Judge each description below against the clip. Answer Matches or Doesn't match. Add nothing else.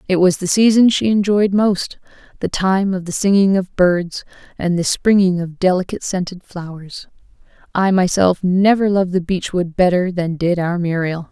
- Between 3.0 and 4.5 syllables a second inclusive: Doesn't match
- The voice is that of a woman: Matches